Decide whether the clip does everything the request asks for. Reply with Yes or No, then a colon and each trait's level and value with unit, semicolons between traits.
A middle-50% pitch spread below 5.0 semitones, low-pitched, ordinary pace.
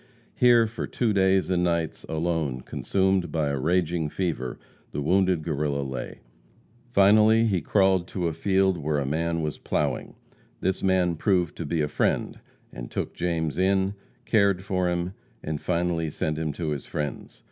Yes: average, 3.6 semitones; very low, 85 Hz; average, 165 wpm